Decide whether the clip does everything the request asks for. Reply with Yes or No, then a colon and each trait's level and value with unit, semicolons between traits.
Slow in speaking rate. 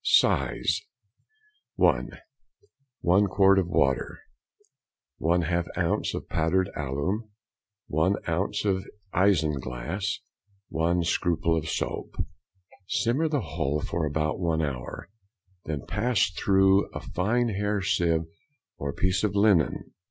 Yes: slow, 110 wpm